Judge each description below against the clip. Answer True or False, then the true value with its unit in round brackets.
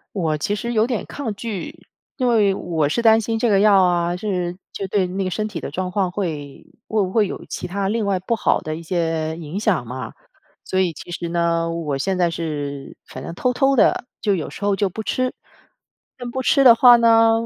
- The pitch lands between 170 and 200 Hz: True (190 Hz)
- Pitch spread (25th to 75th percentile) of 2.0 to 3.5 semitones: False (4.8 semitones)